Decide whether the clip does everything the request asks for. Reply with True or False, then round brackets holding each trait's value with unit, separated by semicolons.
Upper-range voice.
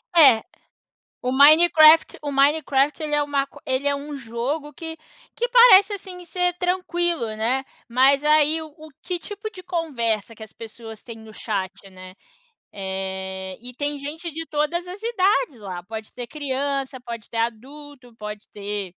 True (280 Hz)